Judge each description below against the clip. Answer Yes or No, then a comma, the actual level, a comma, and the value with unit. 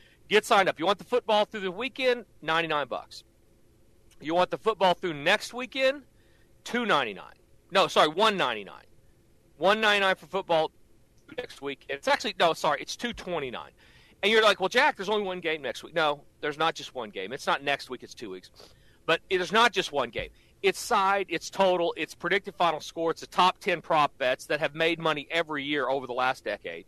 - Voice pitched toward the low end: No, medium, 175 Hz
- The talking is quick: Yes, fast, 215 wpm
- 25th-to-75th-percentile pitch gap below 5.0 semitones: No, wide, 5.6 semitones